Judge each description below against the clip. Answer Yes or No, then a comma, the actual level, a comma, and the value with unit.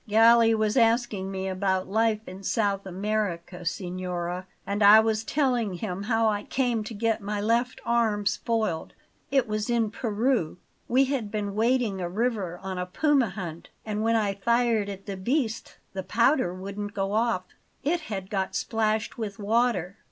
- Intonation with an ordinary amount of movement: Yes, average, 3.2 semitones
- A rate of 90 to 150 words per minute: No, average, 165 wpm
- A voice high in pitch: Yes, high, 215 Hz